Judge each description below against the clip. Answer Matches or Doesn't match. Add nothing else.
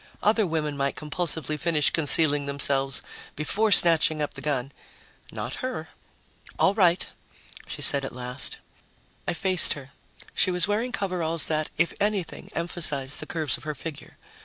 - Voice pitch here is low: Doesn't match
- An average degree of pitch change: Matches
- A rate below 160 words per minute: Matches